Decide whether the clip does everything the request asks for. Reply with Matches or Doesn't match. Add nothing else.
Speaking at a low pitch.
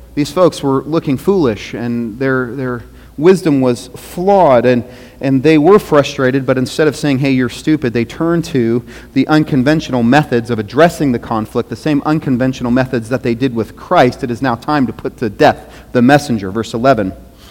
Matches